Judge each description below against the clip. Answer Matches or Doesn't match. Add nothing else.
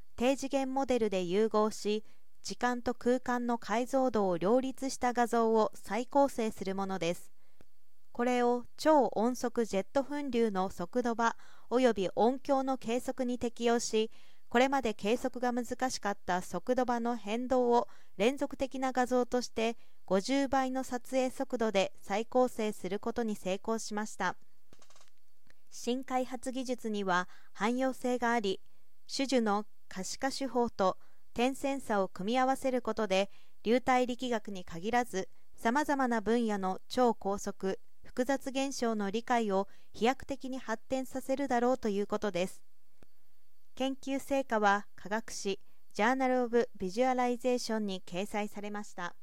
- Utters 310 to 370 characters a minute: Doesn't match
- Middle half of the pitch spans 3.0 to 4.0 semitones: Matches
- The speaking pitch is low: Doesn't match